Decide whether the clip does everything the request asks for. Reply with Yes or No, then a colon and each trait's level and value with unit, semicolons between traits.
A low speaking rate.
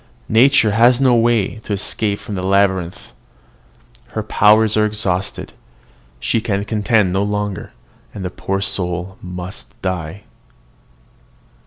Yes: slow, 125 wpm